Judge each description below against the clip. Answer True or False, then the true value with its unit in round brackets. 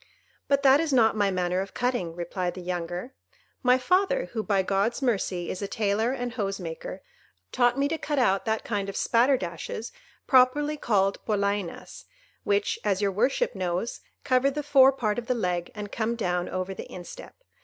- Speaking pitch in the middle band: False (220 Hz)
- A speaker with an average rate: True (180 wpm)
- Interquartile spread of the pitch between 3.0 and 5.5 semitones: True (5.2 semitones)